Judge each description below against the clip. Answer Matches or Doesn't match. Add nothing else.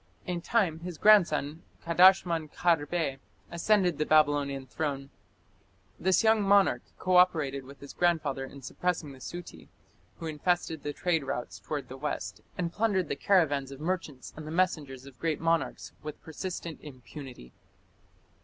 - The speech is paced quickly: Doesn't match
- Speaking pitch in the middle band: Matches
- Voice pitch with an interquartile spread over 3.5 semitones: Matches